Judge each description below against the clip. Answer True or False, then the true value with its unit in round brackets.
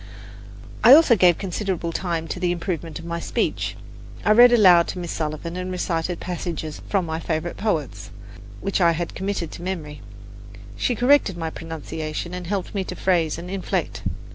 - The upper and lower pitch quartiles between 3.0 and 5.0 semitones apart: False (2.6 semitones)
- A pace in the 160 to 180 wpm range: True (170 wpm)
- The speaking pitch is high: False (175 Hz)